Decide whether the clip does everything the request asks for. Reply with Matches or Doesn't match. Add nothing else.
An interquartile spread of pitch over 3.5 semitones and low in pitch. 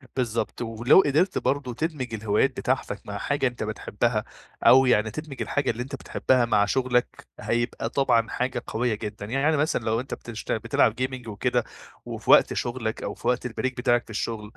Doesn't match